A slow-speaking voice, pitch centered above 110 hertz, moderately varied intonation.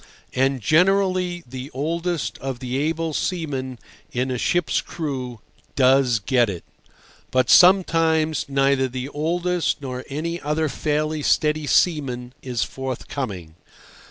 Yes: slow, 120 wpm; medium, 140 Hz; average, 4.2 semitones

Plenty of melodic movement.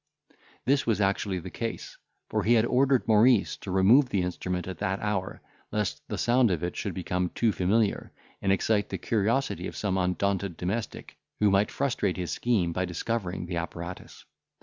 No: average, 3.8 semitones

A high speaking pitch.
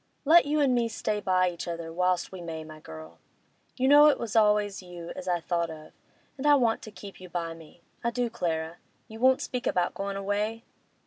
Yes: high, 195 Hz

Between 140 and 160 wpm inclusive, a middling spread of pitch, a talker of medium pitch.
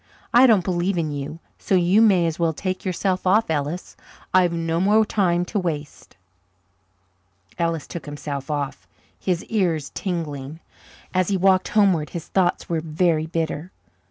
Yes: average, 155 wpm; average, 3.0 semitones; medium, 170 Hz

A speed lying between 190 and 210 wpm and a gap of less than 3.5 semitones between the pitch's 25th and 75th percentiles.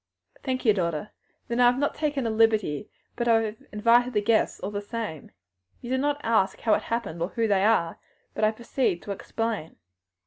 Yes: fast, 205 wpm; average, 2.8 semitones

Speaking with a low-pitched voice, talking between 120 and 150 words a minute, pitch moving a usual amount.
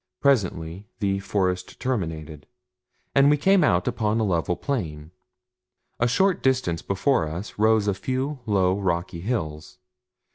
No: low, 100 Hz; slow, 135 wpm; wide, 6.8 semitones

